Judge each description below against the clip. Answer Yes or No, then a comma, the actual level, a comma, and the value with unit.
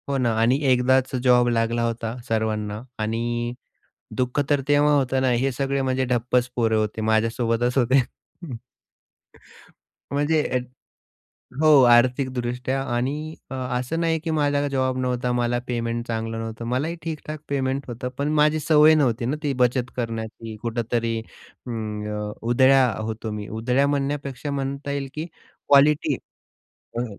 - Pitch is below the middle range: Yes, low, 125 Hz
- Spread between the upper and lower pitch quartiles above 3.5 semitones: No, average, 3.1 semitones